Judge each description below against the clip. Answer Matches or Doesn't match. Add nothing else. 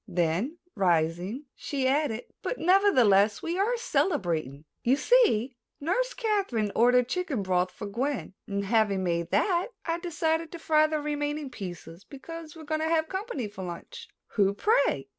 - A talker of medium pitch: Doesn't match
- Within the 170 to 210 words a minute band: Doesn't match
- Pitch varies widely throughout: Matches